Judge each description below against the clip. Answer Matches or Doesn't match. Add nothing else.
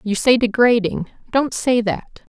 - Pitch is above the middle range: Matches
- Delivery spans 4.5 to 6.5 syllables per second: Doesn't match